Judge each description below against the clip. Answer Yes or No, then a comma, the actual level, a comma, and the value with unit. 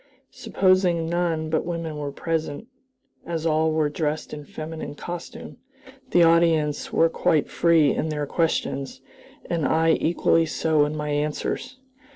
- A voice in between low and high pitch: Yes, medium, 160 Hz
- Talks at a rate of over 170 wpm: No, average, 140 wpm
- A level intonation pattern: Yes, narrow, 1.9 semitones